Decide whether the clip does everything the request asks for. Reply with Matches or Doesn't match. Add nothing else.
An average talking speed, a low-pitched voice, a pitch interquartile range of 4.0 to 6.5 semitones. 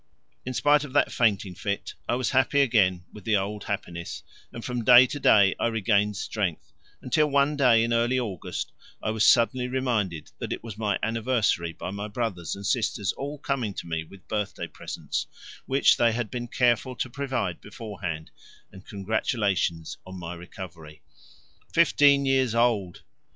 Matches